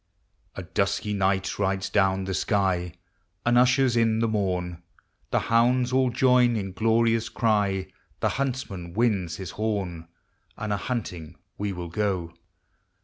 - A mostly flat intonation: No, average, 3.7 semitones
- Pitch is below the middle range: Yes, low, 105 Hz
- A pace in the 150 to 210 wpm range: No, average, 140 wpm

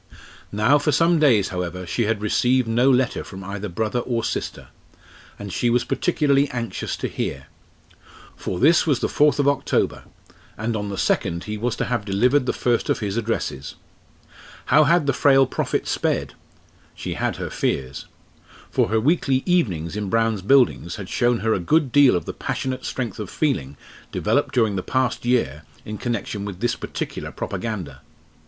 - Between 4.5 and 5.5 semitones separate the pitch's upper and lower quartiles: Yes, average, 4.9 semitones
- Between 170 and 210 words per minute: Yes, average, 175 wpm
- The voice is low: Yes, low, 115 Hz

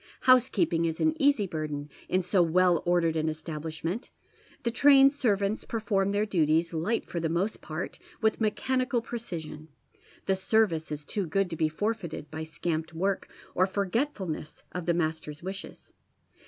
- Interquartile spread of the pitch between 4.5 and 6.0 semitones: Yes, average, 5.1 semitones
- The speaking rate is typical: Yes, average, 165 wpm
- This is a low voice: No, medium, 180 Hz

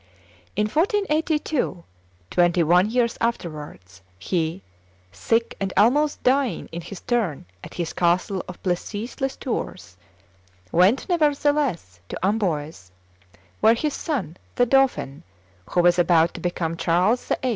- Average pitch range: No, wide, 7.0 semitones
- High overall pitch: Yes, high, 195 Hz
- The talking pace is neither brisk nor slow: No, slow, 125 wpm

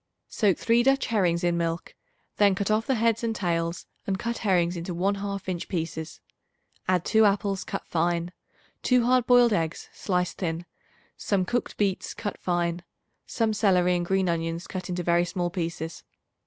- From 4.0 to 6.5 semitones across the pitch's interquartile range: No, average, 3.5 semitones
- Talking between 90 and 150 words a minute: No, average, 170 wpm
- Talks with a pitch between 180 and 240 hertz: Yes, medium, 185 Hz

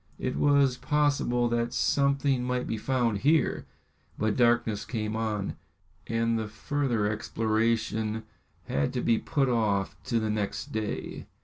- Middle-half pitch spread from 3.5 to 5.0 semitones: No, average, 2.8 semitones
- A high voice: No, low, 115 Hz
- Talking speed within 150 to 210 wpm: No, slow, 135 wpm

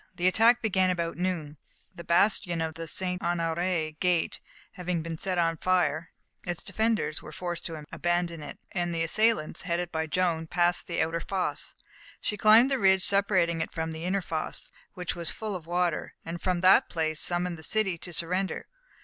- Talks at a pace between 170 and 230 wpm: Yes, average, 185 wpm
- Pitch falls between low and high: Yes, medium, 175 Hz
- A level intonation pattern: Yes, narrow, 2.0 semitones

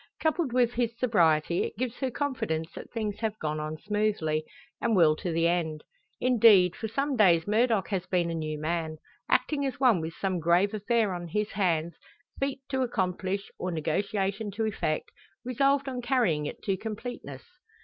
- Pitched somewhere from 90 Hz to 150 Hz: No, high, 200 Hz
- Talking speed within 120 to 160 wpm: No, average, 175 wpm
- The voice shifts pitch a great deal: Yes, wide, 5.9 semitones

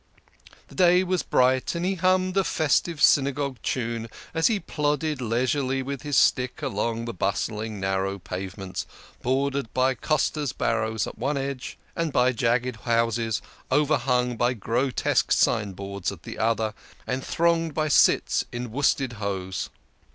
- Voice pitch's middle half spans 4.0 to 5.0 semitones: Yes, average, 4.7 semitones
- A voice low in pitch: Yes, low, 125 Hz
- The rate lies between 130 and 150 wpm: Yes, average, 145 wpm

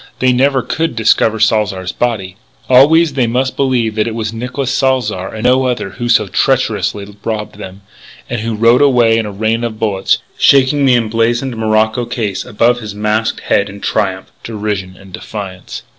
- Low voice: Yes, low, 115 Hz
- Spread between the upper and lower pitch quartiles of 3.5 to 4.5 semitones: No, average, 3.0 semitones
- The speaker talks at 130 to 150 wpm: No, average, 175 wpm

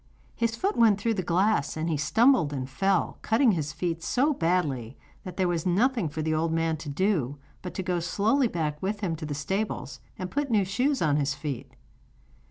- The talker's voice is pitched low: No, medium, 180 Hz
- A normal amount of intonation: No, wide, 5.7 semitones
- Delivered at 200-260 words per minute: Yes, fast, 205 wpm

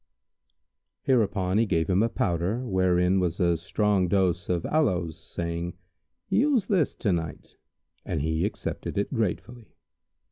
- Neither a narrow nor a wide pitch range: Yes, average, 4.7 semitones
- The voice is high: No, very low, 95 Hz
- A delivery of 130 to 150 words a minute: Yes, slow, 135 wpm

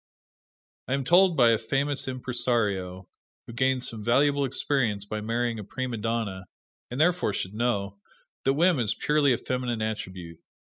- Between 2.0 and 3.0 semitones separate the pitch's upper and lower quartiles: No, average, 4.3 semitones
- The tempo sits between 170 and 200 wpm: No, average, 155 wpm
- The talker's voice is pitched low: Yes, low, 120 Hz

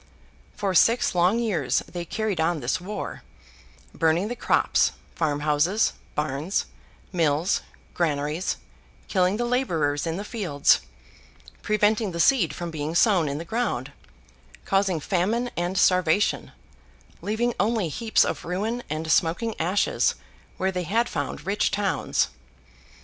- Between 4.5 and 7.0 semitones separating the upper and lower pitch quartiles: Yes, average, 4.8 semitones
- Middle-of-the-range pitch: Yes, medium, 180 Hz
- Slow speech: Yes, slow, 130 wpm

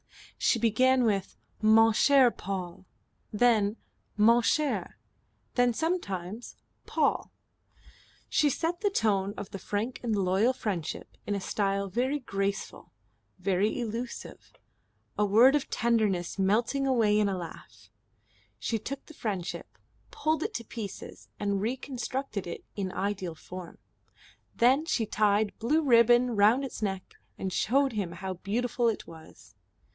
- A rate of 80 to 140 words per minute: Yes, slow, 135 wpm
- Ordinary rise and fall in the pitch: Yes, average, 4.0 semitones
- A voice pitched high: Yes, high, 215 Hz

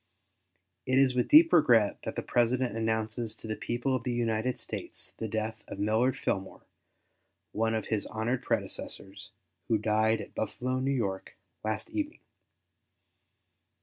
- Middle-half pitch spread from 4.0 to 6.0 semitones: No, average, 2.7 semitones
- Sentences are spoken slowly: No, average, 145 wpm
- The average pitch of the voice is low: Yes, low, 115 Hz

